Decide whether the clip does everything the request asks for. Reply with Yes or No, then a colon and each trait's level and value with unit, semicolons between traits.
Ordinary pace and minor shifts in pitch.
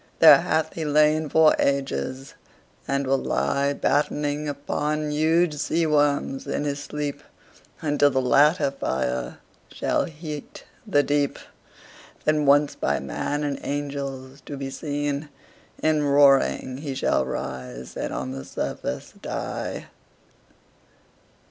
No: slow, 125 wpm; narrow, 1.7 semitones